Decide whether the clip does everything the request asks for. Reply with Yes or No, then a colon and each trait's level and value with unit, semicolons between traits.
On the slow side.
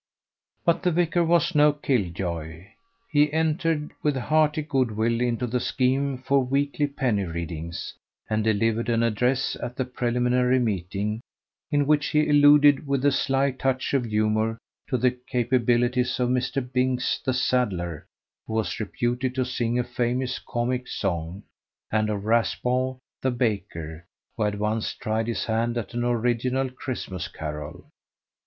No: average, 150 wpm